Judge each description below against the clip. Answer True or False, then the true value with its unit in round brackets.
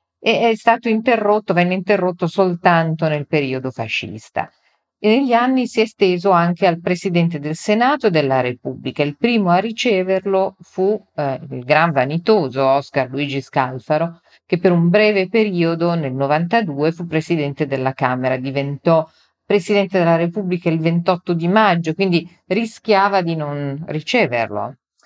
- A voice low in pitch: False (170 Hz)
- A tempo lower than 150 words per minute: True (140 wpm)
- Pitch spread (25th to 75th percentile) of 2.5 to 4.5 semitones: False (5.1 semitones)